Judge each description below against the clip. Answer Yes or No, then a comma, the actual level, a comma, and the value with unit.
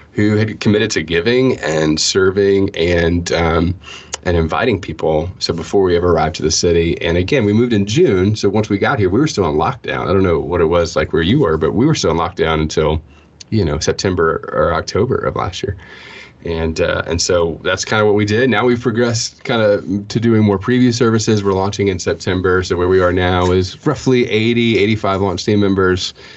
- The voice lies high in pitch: No, very low, 95 Hz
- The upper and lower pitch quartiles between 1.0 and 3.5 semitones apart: No, average, 4.0 semitones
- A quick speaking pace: Yes, fast, 220 wpm